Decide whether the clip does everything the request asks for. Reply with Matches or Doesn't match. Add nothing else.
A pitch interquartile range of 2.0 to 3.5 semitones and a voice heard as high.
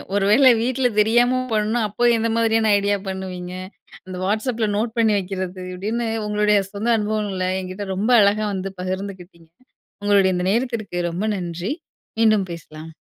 Matches